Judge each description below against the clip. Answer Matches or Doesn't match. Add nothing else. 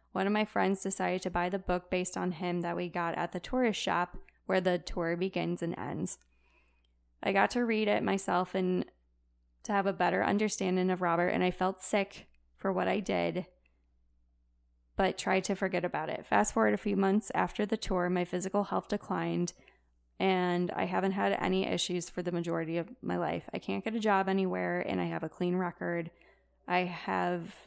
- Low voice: Doesn't match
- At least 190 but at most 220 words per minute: Matches